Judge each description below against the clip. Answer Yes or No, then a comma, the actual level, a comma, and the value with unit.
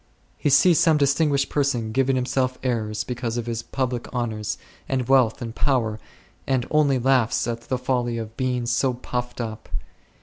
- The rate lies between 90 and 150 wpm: No, average, 165 wpm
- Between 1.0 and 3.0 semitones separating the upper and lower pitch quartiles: Yes, narrow, 2.4 semitones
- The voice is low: Yes, low, 125 Hz